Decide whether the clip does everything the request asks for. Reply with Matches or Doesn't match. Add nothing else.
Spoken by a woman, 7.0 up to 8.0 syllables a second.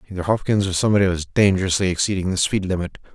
Doesn't match